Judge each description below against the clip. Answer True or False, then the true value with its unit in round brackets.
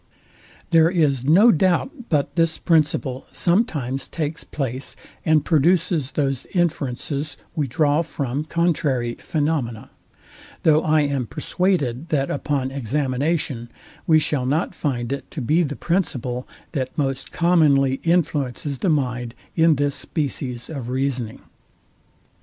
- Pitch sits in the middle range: True (145 Hz)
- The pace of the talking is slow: True (125 wpm)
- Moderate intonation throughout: True (3.7 semitones)